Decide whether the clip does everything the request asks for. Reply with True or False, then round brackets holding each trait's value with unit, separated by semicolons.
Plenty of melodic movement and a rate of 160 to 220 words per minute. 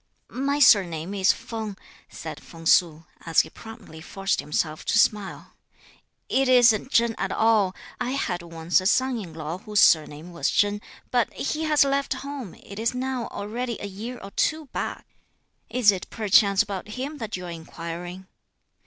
True (5.9 semitones; 170 wpm)